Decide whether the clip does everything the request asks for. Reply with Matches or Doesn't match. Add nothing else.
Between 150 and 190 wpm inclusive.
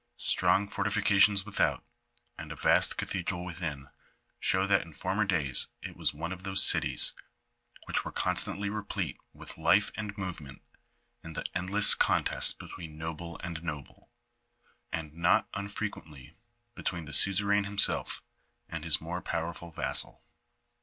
Doesn't match